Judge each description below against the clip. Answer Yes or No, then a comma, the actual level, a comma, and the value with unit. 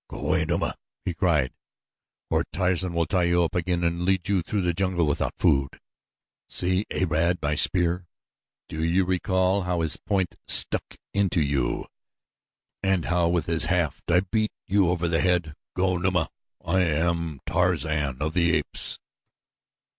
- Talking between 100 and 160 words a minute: Yes, average, 155 wpm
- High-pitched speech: No, very low, 85 Hz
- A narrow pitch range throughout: Yes, narrow, 2.1 semitones